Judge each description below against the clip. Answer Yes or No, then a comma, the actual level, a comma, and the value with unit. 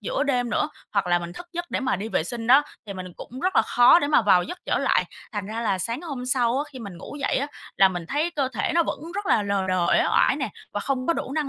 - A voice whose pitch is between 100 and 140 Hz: No, high, 245 Hz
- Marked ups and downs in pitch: Yes, wide, 6.3 semitones